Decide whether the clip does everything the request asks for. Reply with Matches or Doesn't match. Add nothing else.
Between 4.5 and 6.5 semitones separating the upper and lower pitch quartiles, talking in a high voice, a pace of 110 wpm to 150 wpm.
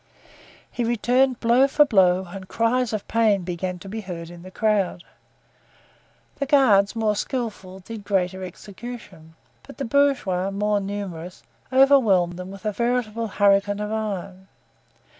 Doesn't match